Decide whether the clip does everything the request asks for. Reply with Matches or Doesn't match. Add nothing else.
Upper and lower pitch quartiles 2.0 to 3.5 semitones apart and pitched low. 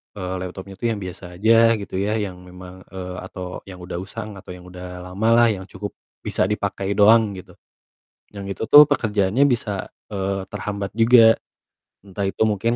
Matches